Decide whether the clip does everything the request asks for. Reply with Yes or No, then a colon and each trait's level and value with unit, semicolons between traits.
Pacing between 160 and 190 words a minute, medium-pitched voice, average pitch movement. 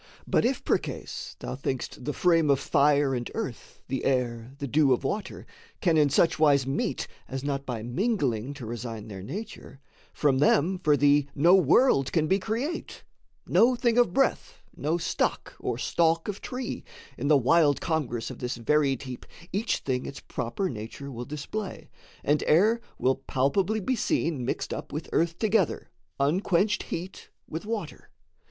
No: average, 165 wpm; medium, 150 Hz; wide, 5.8 semitones